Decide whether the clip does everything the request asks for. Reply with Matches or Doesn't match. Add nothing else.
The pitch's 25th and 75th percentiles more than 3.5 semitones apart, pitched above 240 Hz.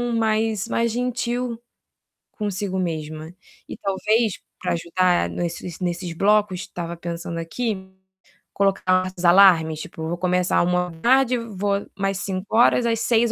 Doesn't match